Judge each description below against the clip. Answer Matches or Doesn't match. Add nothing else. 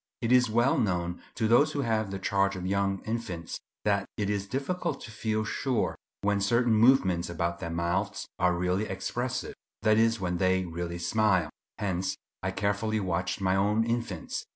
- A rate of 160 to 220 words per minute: Matches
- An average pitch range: Matches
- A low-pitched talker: Matches